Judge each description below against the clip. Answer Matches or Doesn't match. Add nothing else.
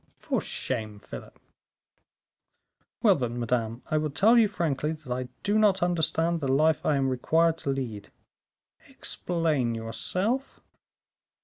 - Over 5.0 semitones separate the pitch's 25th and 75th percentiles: Matches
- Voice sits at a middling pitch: Matches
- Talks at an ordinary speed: Doesn't match